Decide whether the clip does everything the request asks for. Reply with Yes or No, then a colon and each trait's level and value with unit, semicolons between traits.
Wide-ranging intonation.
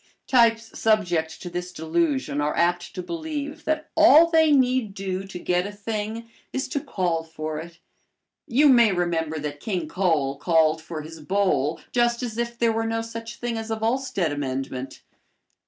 Yes: wide, 6.6 semitones